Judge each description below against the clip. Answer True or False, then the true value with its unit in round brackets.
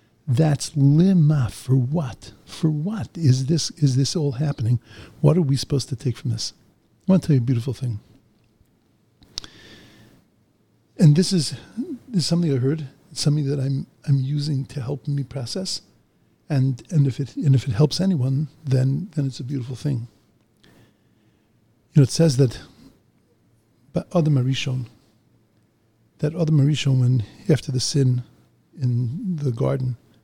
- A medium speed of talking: True (155 wpm)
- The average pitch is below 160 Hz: True (135 Hz)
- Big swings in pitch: False (4.3 semitones)